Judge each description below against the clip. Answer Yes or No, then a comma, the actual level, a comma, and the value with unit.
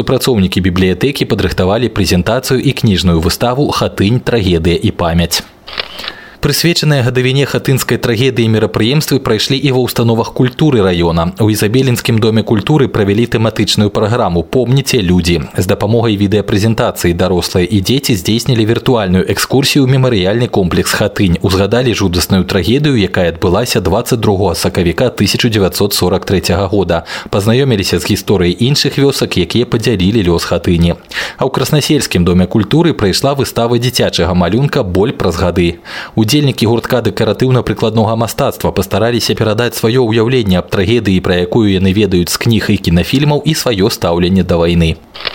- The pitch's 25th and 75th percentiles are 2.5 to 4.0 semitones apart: No, average, 5.2 semitones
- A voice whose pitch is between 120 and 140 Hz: No, low, 110 Hz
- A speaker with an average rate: Yes, average, 130 wpm